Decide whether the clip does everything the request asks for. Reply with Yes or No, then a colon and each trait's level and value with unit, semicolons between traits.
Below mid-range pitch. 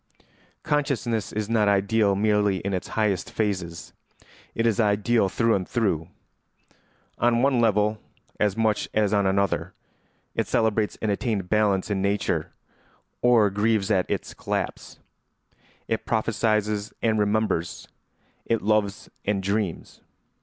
Yes: low, 105 Hz